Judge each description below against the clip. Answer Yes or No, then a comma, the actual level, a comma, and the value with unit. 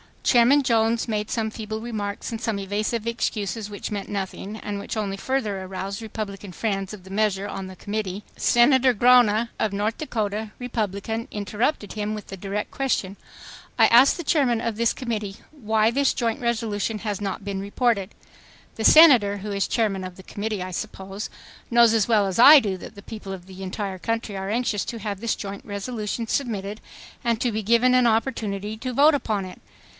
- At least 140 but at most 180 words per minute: No, average, 190 wpm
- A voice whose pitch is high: Yes, high, 215 Hz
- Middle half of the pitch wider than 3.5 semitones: No, average, 2.7 semitones